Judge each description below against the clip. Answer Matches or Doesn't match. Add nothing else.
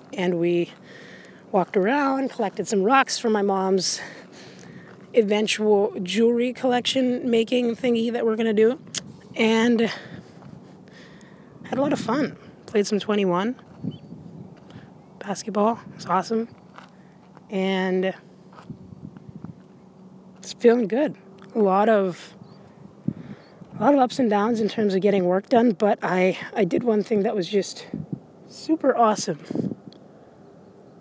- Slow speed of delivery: Matches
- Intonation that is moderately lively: Matches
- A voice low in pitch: Doesn't match